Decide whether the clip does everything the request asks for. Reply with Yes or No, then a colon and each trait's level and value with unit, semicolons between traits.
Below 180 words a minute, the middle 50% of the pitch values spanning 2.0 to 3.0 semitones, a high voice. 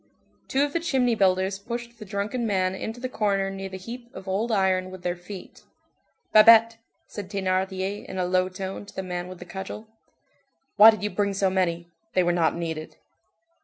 No: average, 195 wpm; average, 2.7 semitones; high, 195 Hz